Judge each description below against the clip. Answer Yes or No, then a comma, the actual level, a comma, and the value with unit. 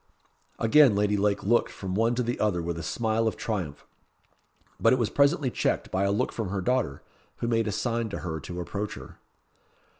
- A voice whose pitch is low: Yes, low, 105 Hz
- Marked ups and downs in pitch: No, average, 3.5 semitones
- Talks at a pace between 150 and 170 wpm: No, fast, 205 wpm